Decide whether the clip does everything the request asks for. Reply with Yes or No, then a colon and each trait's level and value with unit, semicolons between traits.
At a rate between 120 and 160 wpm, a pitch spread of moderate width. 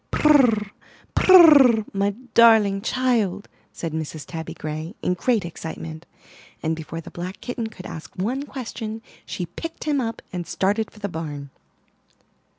No: average, 145 wpm; wide, 6.1 semitones